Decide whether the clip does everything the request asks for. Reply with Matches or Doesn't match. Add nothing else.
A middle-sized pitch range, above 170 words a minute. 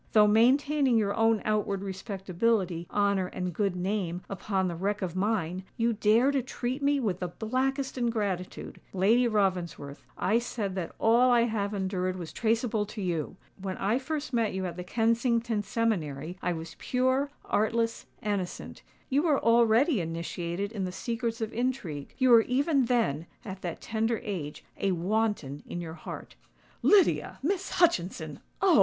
Doesn't match